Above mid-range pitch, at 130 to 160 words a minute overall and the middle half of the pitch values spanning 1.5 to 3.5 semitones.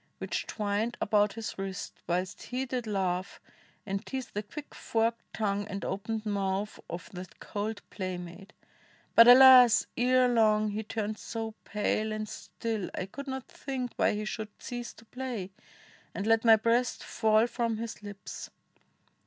Yes: high, 215 Hz; average, 155 wpm; average, 2.7 semitones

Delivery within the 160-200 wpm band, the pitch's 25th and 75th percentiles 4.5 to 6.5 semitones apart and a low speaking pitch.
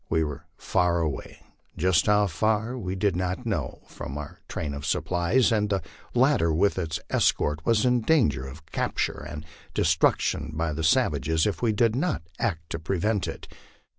Yes: average, 170 wpm; wide, 5.6 semitones; very low, 90 Hz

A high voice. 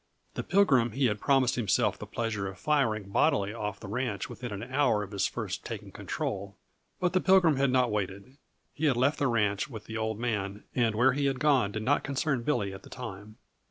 No: low, 115 Hz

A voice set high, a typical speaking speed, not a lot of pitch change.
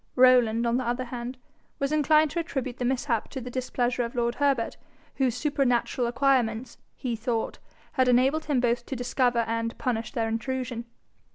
Yes: high, 245 Hz; average, 170 wpm; narrow, 1.9 semitones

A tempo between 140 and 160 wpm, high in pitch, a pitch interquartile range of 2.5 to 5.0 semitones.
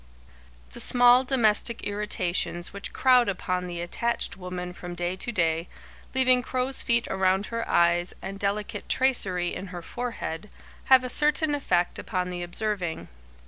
No: average, 145 wpm; high, 200 Hz; wide, 5.5 semitones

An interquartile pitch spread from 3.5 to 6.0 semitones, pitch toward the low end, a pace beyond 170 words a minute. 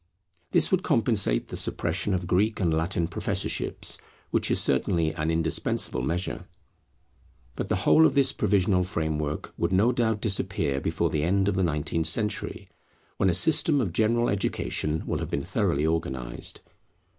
No: average, 5.0 semitones; very low, 90 Hz; average, 155 wpm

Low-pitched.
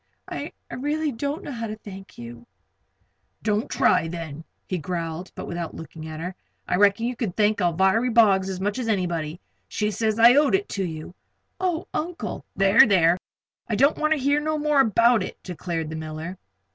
No: high, 200 Hz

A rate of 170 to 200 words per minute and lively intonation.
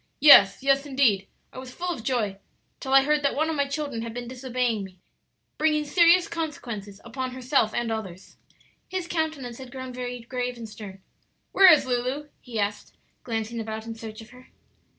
No: average, 185 wpm; average, 4.0 semitones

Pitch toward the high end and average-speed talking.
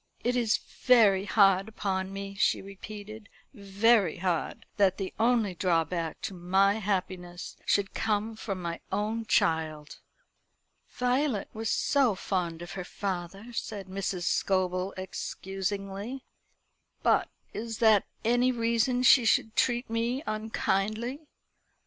No: high, 200 Hz; slow, 120 wpm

